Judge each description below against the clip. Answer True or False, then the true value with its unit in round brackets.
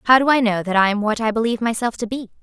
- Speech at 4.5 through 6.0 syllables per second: False (7.4 syllables/s)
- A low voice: False (225 Hz)